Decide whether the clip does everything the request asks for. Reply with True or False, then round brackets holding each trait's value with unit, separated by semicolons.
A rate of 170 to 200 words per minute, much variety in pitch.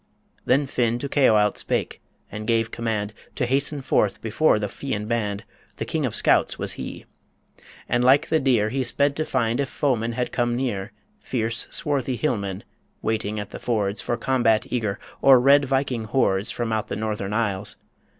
False (175 wpm; 3.7 semitones)